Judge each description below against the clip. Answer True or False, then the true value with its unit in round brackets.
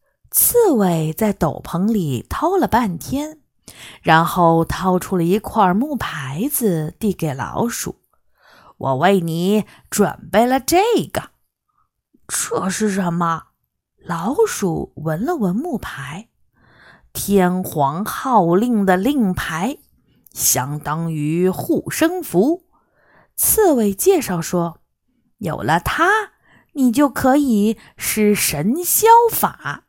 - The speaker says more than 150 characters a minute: False (145 characters per minute)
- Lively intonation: True (8.2 semitones)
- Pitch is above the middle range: True (205 Hz)